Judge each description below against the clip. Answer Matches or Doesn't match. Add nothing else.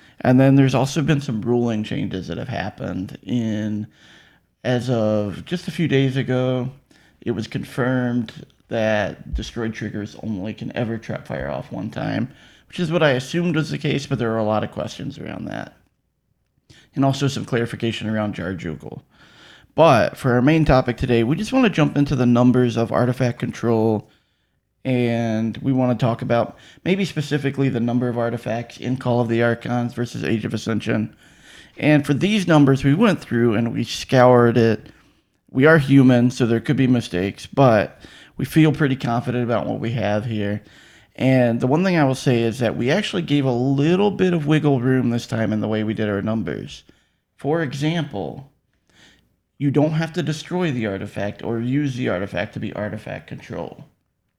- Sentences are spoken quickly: Doesn't match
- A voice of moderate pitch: Doesn't match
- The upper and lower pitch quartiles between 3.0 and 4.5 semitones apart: Matches